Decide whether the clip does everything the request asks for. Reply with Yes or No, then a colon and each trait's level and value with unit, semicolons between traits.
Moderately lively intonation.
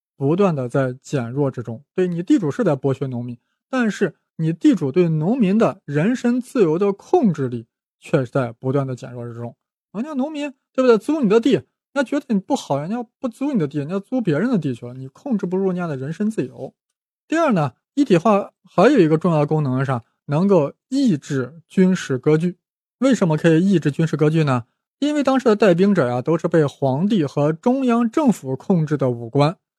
No: wide, 8.1 semitones